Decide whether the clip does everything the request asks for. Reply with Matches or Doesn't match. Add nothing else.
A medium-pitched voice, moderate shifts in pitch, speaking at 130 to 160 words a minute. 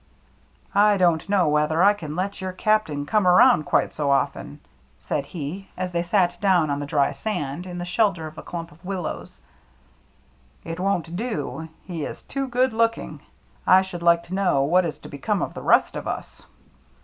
Doesn't match